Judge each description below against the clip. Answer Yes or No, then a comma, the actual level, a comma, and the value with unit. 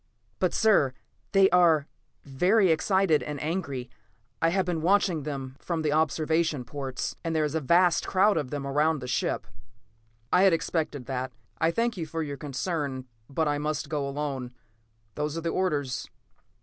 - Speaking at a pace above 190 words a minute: No, average, 170 wpm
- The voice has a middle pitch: Yes, medium, 155 Hz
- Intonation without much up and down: No, average, 3.5 semitones